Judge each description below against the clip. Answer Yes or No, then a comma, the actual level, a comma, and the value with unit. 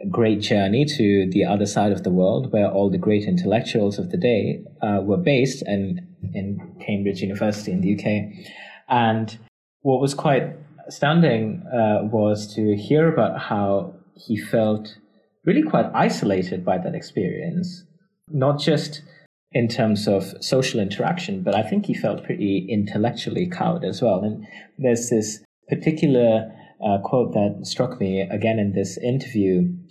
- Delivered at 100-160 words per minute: Yes, average, 150 wpm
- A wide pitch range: Yes, wide, 6.9 semitones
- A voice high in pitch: No, low, 110 Hz